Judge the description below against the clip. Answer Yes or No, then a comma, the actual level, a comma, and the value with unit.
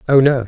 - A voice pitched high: No, low, 130 Hz